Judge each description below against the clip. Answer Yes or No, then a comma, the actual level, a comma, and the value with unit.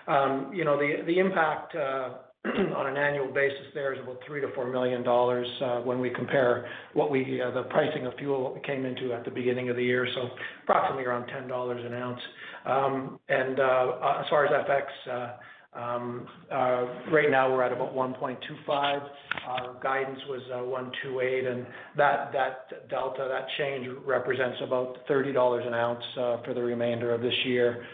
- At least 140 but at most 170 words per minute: No, average, 185 wpm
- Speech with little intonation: Yes, narrow, 1.8 semitones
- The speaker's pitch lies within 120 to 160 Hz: Yes, low, 125 Hz